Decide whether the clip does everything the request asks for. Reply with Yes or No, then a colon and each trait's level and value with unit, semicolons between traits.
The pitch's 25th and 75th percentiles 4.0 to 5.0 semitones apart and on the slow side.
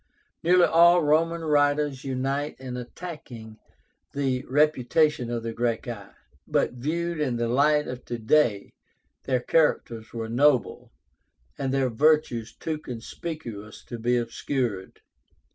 Yes: average, 4.4 semitones; slow, 125 wpm